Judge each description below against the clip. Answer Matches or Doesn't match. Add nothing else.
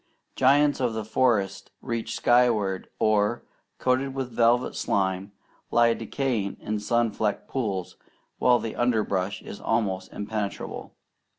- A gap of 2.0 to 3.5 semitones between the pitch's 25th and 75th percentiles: Matches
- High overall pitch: Doesn't match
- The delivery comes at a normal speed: Doesn't match